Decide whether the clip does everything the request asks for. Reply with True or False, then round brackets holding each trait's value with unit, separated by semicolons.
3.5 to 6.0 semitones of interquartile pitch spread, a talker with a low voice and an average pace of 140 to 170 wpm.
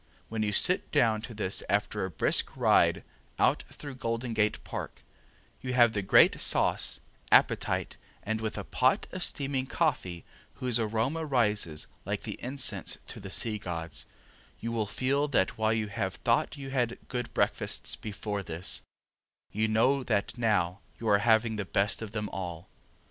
True (3.8 semitones; 110 Hz; 165 wpm)